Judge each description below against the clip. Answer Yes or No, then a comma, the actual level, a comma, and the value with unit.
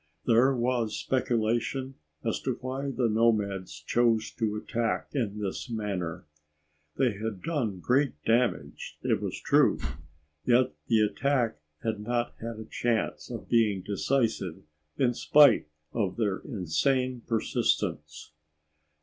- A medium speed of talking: No, slow, 125 wpm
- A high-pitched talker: No, low, 115 Hz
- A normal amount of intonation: Yes, average, 3.3 semitones